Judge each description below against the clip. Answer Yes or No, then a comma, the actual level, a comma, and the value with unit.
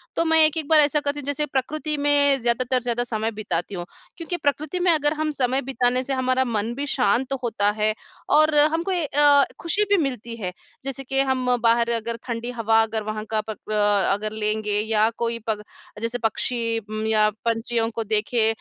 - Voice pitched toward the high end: Yes, high, 245 Hz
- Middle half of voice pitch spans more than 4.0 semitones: Yes, average, 4.6 semitones